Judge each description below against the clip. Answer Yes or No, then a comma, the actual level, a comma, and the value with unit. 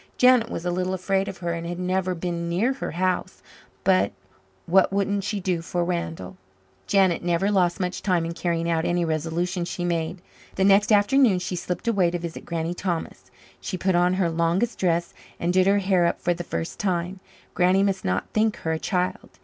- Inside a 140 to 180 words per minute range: No, average, 200 wpm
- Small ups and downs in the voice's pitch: Yes, narrow, 2.2 semitones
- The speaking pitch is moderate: Yes, medium, 180 Hz